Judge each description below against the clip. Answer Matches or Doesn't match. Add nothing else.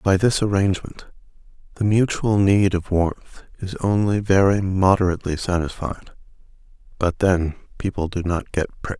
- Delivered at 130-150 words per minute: Matches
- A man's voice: Matches